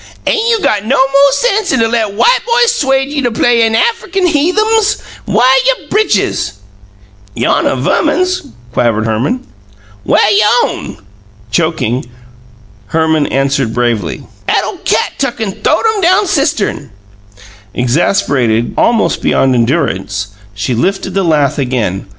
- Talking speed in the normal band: No, slow, 130 wpm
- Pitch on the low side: No, high, 215 Hz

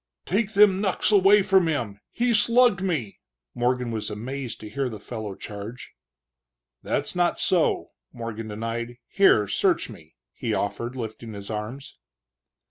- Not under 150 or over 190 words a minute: No, average, 140 wpm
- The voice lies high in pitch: No, low, 120 Hz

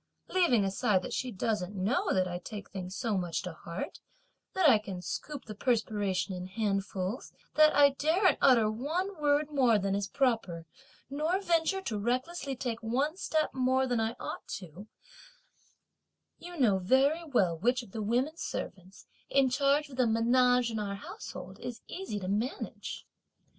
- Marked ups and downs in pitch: Yes, wide, 6.1 semitones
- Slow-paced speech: No, average, 165 wpm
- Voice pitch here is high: Yes, high, 235 Hz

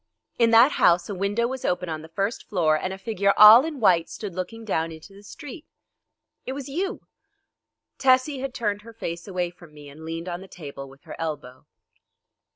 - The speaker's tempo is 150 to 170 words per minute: No, average, 200 wpm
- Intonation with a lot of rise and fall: Yes, wide, 5.9 semitones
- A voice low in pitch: No, high, 195 Hz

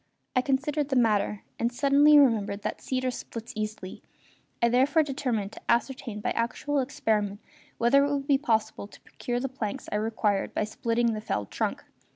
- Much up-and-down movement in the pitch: No, average, 4.2 semitones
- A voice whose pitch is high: Yes, high, 240 Hz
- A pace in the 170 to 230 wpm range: Yes, average, 175 wpm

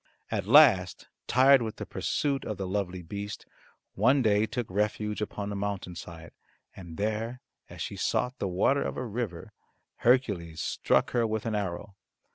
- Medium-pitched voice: No, low, 105 Hz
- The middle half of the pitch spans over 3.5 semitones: Yes, average, 3.9 semitones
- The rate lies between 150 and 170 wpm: Yes, average, 160 wpm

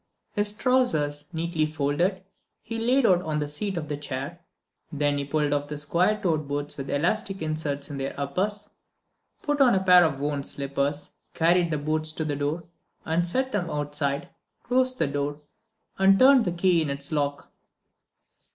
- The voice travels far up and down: No, average, 4.7 semitones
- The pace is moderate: Yes, average, 170 wpm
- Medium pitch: Yes, medium, 155 Hz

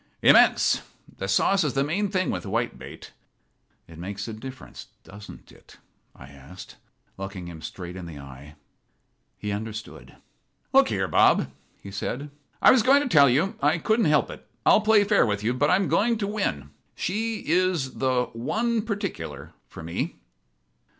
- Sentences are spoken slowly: No, average, 165 wpm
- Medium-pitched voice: No, low, 130 Hz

